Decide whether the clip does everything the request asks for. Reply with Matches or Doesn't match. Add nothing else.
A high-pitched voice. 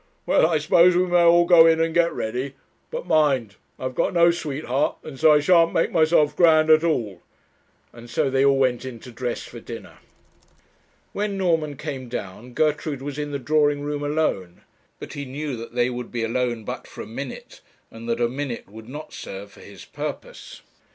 Doesn't match